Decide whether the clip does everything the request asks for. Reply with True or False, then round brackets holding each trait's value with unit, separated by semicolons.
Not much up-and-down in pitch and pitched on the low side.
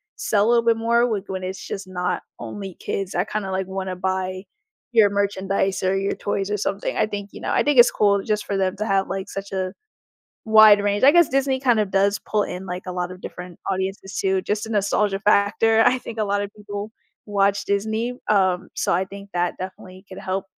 False (1.9 semitones; 200 Hz)